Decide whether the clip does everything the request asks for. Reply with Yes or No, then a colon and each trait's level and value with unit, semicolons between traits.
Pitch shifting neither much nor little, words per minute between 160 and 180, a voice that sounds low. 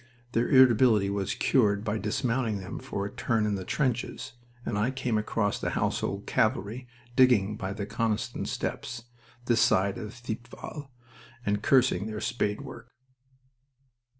No: average, 3.2 semitones; average, 145 wpm; low, 110 Hz